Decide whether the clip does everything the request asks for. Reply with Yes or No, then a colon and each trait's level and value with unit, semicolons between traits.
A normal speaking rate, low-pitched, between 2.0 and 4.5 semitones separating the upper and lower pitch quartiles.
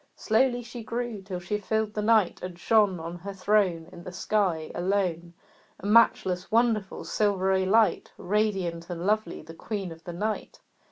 No: average, 165 wpm; high, 195 Hz; average, 3.6 semitones